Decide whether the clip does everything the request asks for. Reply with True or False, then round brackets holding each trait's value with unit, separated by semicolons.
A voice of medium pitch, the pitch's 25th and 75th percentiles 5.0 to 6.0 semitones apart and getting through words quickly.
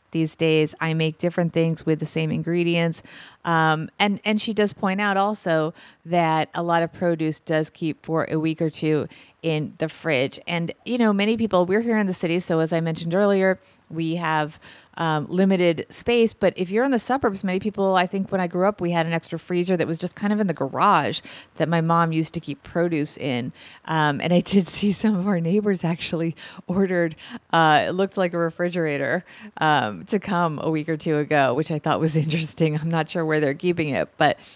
False (170 Hz; 3.2 semitones; 220 wpm)